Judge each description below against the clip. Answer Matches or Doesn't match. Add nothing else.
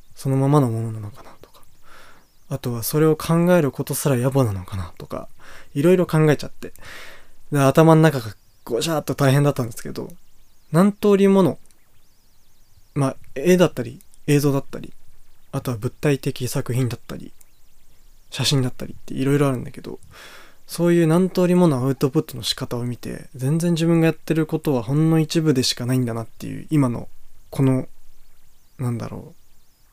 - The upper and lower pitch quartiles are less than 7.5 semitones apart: Matches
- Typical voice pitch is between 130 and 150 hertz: Matches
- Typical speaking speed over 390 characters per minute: Doesn't match